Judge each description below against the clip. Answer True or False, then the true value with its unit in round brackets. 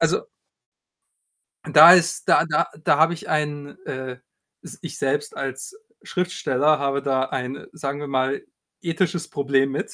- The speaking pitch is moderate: True (145 Hz)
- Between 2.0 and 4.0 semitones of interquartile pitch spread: True (2.8 semitones)